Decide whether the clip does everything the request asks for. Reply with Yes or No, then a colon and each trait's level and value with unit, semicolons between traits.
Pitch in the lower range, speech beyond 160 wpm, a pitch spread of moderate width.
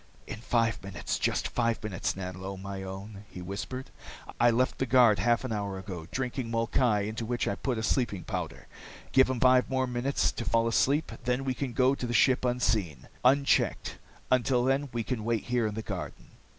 Yes: low, 115 Hz; average, 195 wpm; average, 3.9 semitones